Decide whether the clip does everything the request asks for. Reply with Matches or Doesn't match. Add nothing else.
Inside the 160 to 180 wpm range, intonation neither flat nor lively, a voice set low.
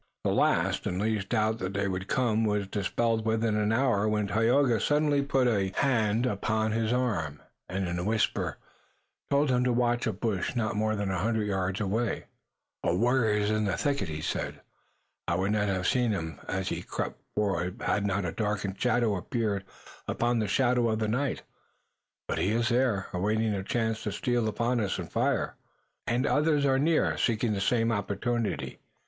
Doesn't match